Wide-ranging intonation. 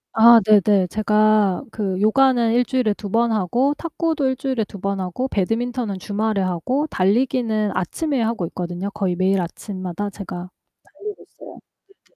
No: average, 4.3 semitones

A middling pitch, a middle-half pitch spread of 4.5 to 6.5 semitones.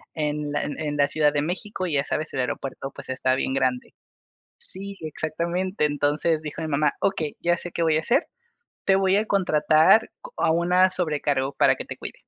No: medium, 155 Hz; average, 3.6 semitones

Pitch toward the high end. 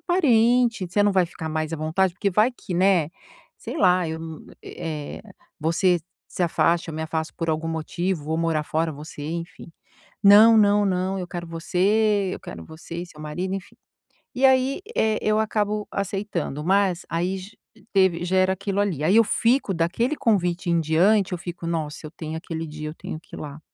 No: medium, 180 Hz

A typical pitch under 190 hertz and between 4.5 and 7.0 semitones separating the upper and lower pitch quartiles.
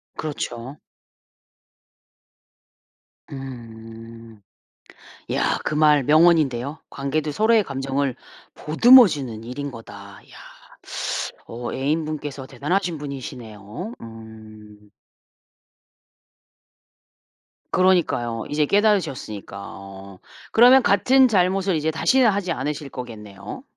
Yes: medium, 140 Hz; wide, 6.5 semitones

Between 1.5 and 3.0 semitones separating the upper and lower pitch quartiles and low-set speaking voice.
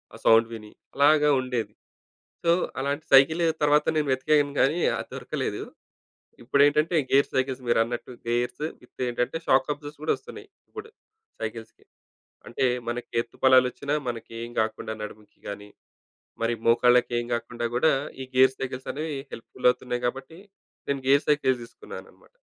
No: average, 3.6 semitones; low, 130 Hz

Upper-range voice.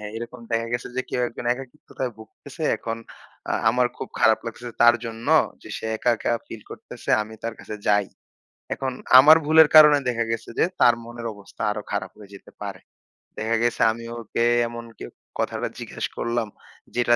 No: low, 115 Hz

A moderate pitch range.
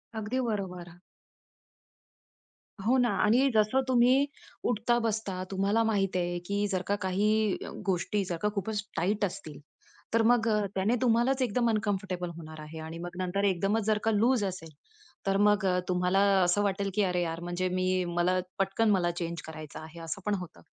Yes: average, 3.5 semitones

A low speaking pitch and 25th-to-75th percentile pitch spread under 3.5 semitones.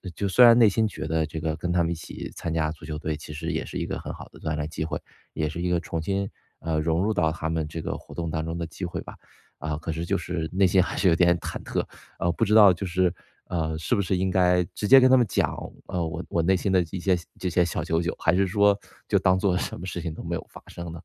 Yes: very low, 85 Hz; average, 2.8 semitones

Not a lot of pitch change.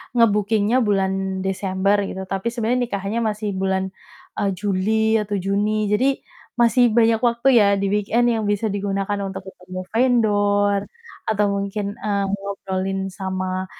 Yes: narrow, 2.3 semitones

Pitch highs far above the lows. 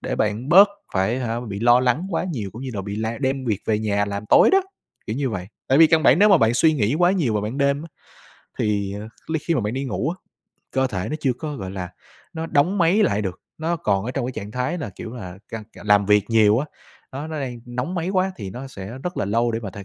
Yes: wide, 6.3 semitones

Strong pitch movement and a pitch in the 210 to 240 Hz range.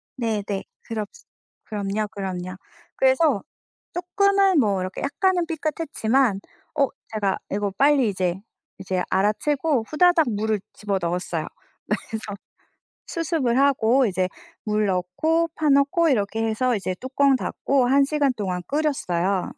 Yes: wide, 6.4 semitones; high, 225 Hz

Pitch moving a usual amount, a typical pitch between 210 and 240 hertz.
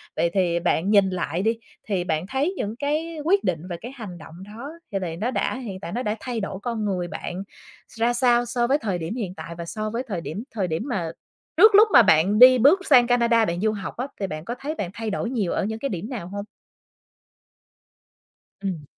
Yes: average, 5.0 semitones; high, 215 Hz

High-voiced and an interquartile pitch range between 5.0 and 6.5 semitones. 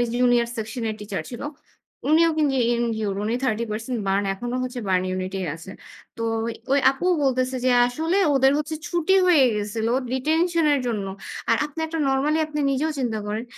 Yes: very high, 250 Hz; average, 5.3 semitones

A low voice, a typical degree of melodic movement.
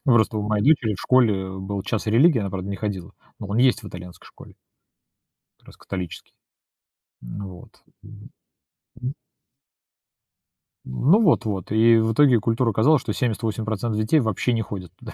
Yes: low, 110 Hz; average, 3.6 semitones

